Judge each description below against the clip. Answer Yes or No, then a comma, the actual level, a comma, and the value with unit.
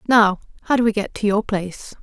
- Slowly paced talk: No, fast, 235 wpm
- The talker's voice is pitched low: No, high, 210 Hz